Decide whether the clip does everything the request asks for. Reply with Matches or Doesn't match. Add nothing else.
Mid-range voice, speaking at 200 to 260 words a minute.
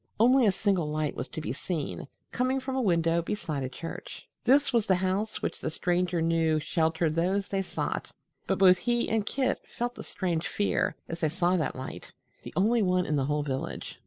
Matches